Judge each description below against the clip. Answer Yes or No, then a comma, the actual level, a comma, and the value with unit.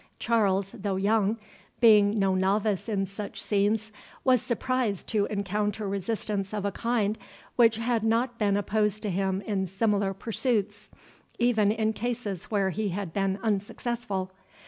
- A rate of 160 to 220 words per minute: No, average, 145 wpm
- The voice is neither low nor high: No, high, 210 Hz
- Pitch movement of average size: No, narrow, 2.2 semitones